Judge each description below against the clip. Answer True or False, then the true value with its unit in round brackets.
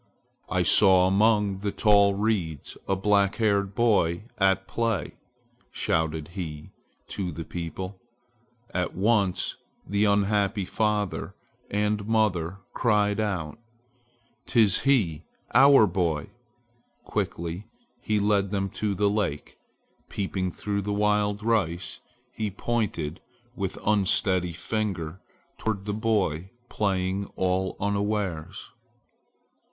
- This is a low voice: True (100 Hz)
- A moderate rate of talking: False (105 wpm)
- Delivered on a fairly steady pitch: True (2.3 semitones)